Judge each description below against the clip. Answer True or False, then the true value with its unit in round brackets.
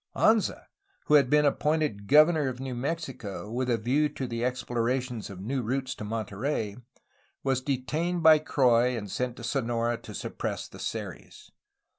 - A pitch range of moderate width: True (3.8 semitones)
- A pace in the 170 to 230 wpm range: False (160 wpm)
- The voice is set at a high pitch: False (125 Hz)